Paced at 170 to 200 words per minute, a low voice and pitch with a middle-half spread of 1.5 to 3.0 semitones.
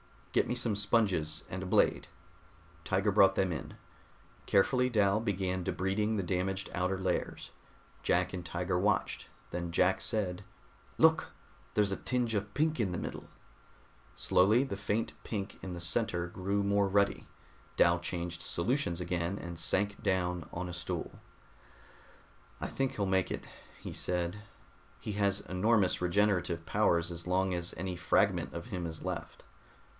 No: average, 150 wpm; very low, 95 Hz; average, 2.7 semitones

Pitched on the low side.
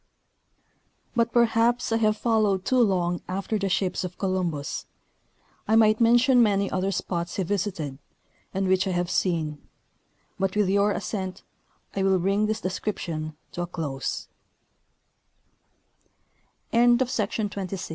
No: high, 195 Hz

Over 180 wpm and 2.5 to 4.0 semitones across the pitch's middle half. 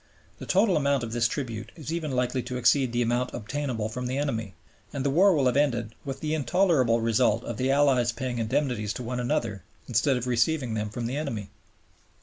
Yes: fast, 205 wpm; average, 3.5 semitones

